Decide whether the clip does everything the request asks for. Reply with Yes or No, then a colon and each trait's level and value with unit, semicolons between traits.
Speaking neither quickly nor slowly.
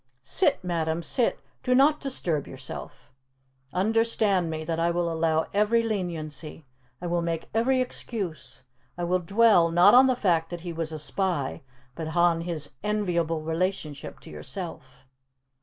Yes: average, 150 wpm